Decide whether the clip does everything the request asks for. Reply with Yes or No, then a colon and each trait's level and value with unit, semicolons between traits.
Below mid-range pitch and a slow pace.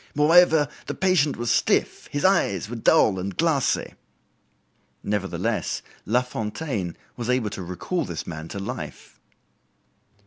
Yes: low, 120 Hz; slow, 125 wpm